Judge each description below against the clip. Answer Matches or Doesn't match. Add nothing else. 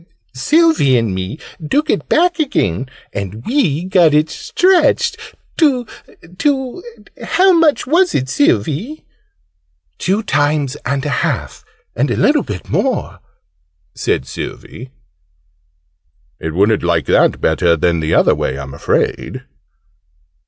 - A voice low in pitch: Doesn't match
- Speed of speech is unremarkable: Doesn't match